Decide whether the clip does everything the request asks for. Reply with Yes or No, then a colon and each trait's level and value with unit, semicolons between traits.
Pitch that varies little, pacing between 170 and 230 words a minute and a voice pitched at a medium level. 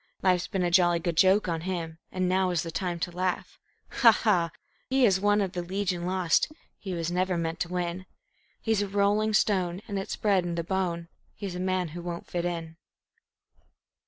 Yes: narrow, 2.0 semitones; average, 200 wpm; medium, 180 Hz